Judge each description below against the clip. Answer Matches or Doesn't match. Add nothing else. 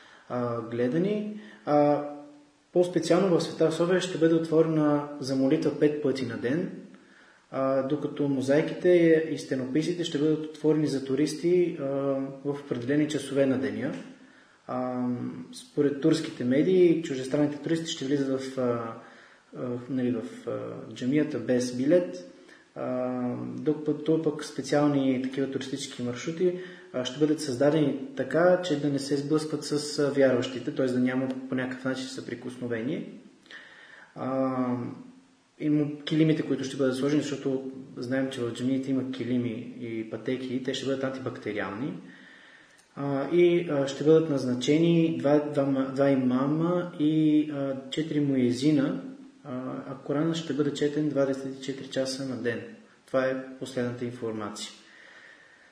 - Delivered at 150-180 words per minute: Doesn't match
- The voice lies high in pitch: Doesn't match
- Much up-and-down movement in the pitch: Doesn't match